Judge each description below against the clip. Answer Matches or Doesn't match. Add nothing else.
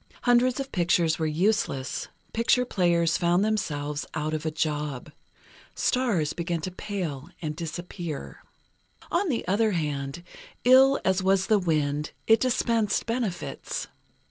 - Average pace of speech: Doesn't match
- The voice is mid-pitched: Matches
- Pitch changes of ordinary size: Doesn't match